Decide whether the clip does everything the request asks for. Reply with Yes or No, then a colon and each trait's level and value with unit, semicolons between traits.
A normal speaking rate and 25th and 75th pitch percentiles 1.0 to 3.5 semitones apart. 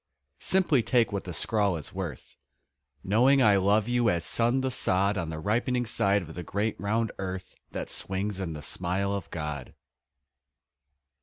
No: average, 165 wpm; average, 4.1 semitones